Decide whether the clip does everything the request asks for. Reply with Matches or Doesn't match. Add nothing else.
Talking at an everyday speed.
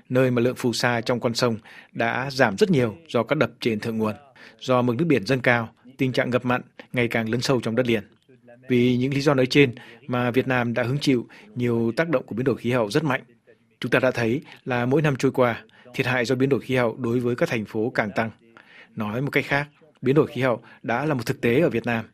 Doesn't match